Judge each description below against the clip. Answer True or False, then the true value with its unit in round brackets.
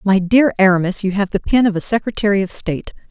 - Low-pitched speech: False (200 Hz)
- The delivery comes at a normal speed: False (230 wpm)